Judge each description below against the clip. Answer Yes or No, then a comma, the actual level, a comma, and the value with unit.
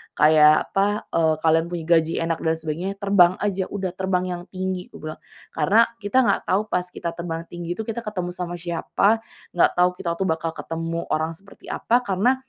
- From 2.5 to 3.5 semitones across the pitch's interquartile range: Yes, average, 3.1 semitones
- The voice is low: No, medium, 175 Hz